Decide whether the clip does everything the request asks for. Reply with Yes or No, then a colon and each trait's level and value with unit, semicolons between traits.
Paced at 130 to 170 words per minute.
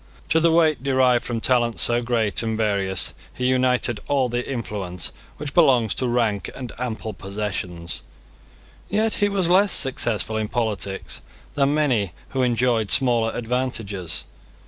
Yes: average, 145 wpm